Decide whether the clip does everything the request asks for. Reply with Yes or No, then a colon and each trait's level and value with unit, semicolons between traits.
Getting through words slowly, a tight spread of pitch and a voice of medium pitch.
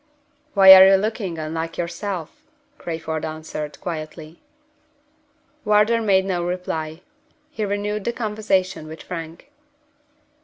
No: slow, 110 wpm; average, 4.2 semitones; medium, 180 Hz